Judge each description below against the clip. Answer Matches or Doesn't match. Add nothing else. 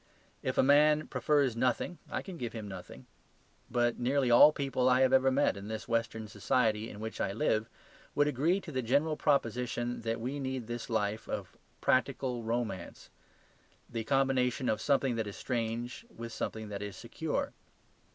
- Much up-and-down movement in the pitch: Doesn't match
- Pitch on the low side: Matches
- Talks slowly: Doesn't match